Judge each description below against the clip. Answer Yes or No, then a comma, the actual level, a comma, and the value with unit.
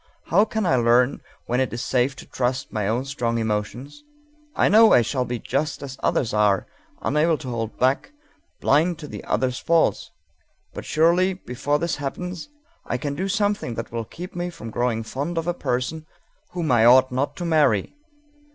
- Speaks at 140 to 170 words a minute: No, average, 185 wpm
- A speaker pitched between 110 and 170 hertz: Yes, low, 135 Hz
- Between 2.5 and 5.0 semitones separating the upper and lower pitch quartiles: No, wide, 5.6 semitones